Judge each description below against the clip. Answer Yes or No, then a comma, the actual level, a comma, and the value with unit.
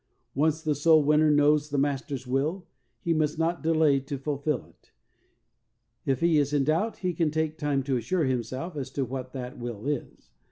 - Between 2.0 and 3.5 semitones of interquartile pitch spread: Yes, average, 2.8 semitones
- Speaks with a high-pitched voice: No, medium, 145 Hz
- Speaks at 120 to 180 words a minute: No, average, 190 wpm